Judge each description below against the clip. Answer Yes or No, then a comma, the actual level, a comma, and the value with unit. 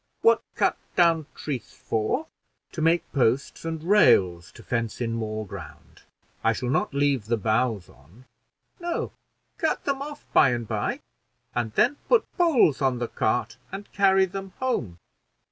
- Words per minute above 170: No, average, 155 wpm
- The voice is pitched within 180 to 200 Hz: No, low, 135 Hz